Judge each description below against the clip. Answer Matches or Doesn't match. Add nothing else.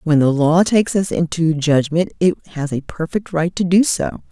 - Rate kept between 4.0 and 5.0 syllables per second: Matches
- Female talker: Matches